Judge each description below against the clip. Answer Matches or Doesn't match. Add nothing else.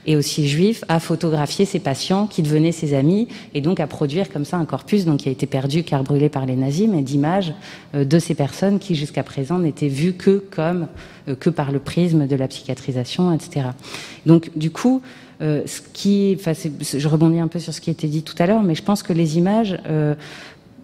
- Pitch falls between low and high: Matches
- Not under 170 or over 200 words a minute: Doesn't match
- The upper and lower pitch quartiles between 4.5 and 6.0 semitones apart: Doesn't match